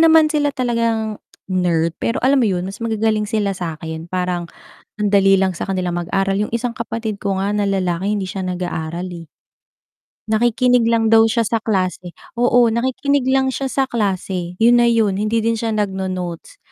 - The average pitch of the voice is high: Yes, high, 210 Hz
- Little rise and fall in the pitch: No, average, 4.0 semitones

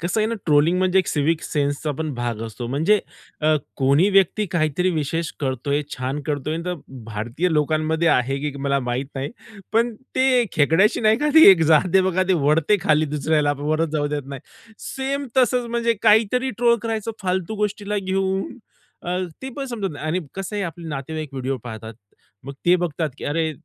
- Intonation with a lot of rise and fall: Yes, wide, 5.7 semitones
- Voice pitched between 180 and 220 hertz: No, medium, 165 Hz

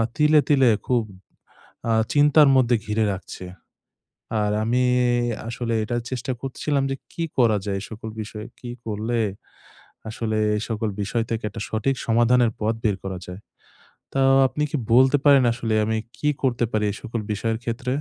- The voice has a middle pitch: No, low, 115 Hz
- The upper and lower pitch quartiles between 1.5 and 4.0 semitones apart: Yes, average, 3.0 semitones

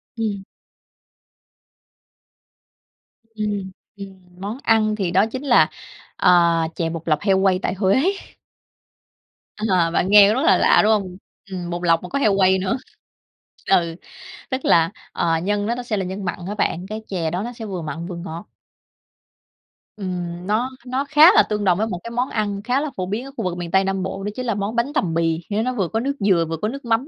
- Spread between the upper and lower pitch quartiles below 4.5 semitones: Yes, average, 3.8 semitones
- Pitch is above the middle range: Yes, high, 195 Hz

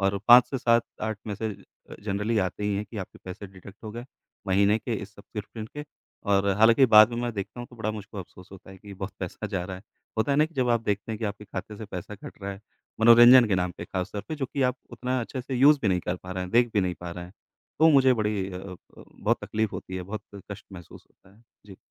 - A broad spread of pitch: No, average, 3.5 semitones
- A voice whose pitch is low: Yes, low, 105 Hz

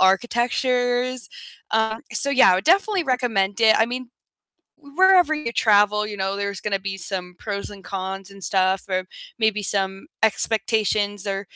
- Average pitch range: Yes, average, 4.0 semitones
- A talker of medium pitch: No, high, 210 Hz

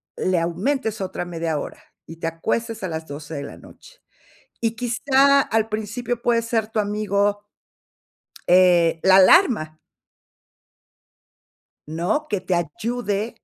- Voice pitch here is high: Yes, high, 205 Hz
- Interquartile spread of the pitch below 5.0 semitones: No, average, 5.3 semitones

